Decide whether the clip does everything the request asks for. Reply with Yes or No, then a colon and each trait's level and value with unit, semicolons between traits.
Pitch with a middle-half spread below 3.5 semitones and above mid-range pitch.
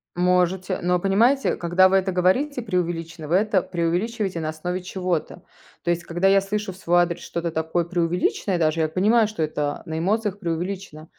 No: average, 2.7 semitones; medium, 180 Hz